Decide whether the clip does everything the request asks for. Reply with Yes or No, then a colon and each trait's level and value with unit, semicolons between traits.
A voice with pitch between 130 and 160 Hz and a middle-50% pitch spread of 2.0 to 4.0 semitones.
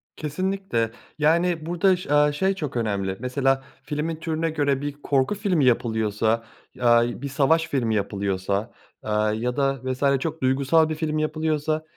No: medium, 140 Hz; average, 5.2 semitones